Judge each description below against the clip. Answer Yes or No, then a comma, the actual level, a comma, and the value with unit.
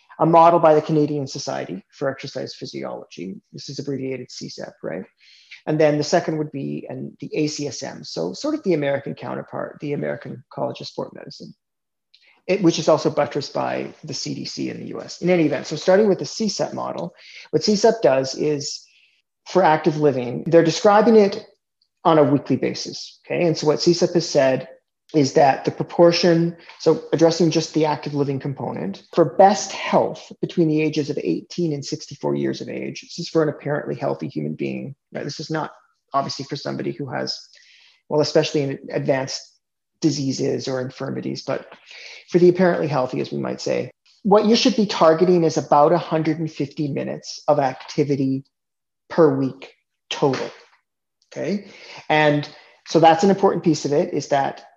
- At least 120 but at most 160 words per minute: No, average, 175 wpm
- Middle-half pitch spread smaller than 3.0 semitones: No, average, 3.6 semitones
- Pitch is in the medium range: Yes, medium, 155 Hz